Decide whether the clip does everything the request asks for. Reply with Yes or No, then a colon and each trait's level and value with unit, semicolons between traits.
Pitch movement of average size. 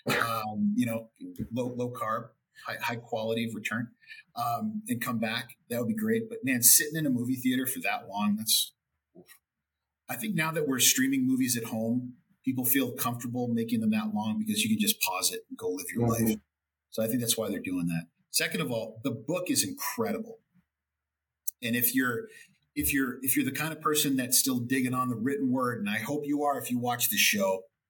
No: wide, 8.3 semitones